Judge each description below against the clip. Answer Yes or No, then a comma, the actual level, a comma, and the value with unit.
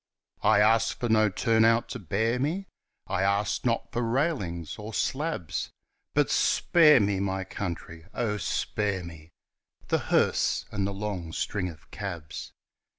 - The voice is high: No, low, 105 Hz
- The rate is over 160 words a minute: No, average, 150 wpm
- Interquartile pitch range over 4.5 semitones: No, average, 3.9 semitones